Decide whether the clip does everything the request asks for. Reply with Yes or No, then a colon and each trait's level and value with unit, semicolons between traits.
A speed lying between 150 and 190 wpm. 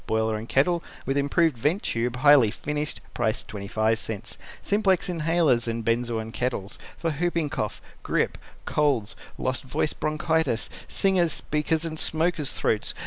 No: slow, 135 wpm